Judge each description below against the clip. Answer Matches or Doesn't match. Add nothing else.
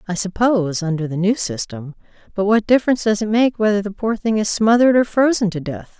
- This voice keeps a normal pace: Doesn't match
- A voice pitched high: Matches